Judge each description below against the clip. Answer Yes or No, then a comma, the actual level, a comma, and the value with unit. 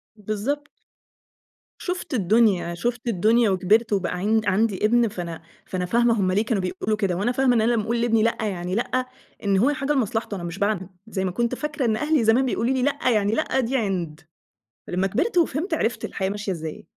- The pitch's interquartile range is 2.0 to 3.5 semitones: No, average, 4.2 semitones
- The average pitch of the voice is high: Yes, high, 220 Hz